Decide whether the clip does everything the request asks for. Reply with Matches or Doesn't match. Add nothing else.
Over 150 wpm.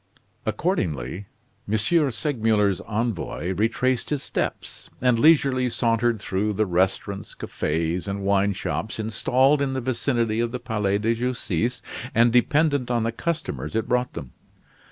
Doesn't match